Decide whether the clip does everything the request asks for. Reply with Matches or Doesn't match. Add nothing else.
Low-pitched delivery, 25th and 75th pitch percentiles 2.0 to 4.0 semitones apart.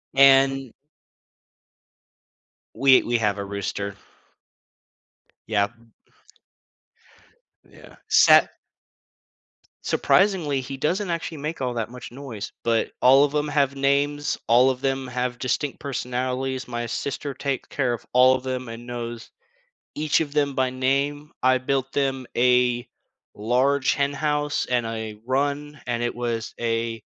Matches